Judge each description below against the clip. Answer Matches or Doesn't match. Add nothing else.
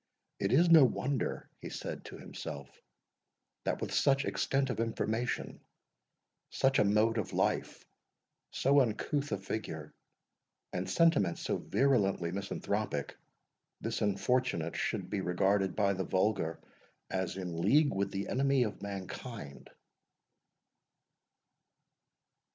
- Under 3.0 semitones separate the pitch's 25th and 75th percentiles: Doesn't match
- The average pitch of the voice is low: Matches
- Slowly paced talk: Matches